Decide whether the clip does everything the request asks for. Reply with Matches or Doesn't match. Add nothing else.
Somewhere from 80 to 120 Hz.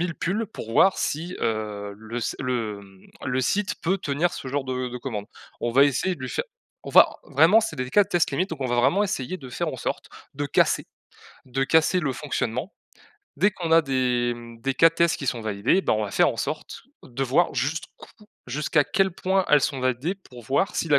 Doesn't match